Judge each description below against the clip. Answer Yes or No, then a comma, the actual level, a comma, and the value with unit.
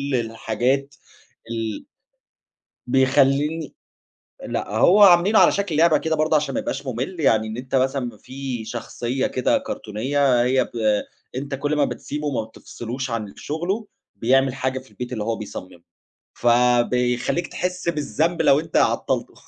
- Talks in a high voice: No, low, 135 Hz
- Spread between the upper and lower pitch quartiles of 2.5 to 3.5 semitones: No, average, 4.2 semitones